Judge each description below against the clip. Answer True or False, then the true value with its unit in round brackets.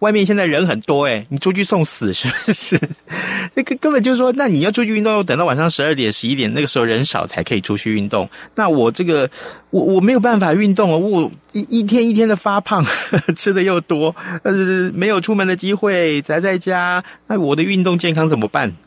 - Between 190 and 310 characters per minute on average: False (320 characters per minute)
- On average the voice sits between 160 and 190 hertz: True (185 Hz)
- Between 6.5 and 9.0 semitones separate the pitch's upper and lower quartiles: False (5.1 semitones)